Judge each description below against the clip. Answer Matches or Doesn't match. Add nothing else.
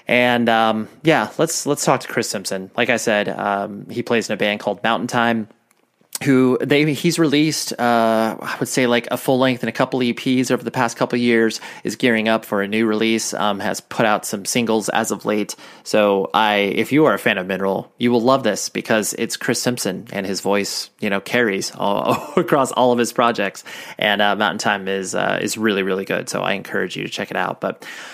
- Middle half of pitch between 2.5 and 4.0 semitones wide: Matches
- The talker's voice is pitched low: Matches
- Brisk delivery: Matches